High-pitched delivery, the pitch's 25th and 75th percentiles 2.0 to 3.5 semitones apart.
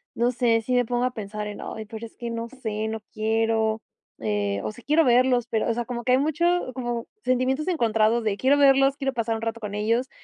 Yes: high, 235 Hz; narrow, 2.6 semitones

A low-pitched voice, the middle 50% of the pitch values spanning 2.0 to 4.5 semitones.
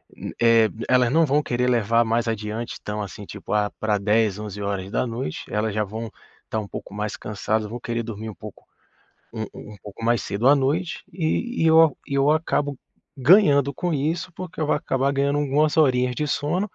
No: low, 120 Hz; average, 5.1 semitones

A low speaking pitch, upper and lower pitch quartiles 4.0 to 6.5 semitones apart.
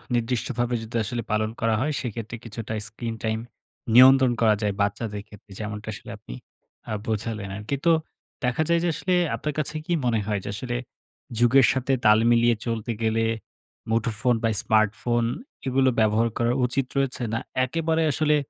No: low, 115 Hz; average, 2.8 semitones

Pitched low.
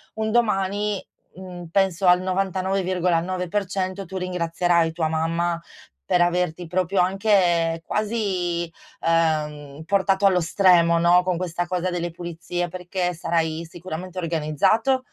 No: medium, 180 Hz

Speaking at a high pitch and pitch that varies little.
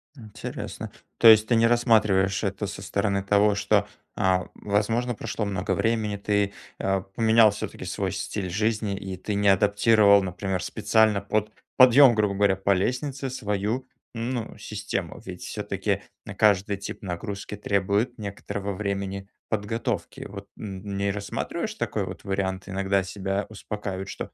No: low, 100 Hz; narrow, 1.9 semitones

